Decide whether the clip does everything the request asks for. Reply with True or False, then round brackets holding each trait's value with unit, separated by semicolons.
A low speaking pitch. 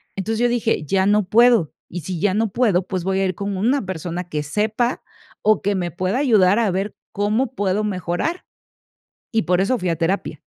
False (200 Hz)